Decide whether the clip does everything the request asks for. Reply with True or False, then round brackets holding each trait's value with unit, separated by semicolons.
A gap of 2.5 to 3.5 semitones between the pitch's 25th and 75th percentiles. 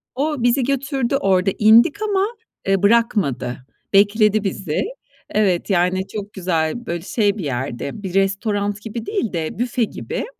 False (4.4 semitones)